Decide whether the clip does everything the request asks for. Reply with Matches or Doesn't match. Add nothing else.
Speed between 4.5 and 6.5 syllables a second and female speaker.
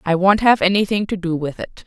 Matches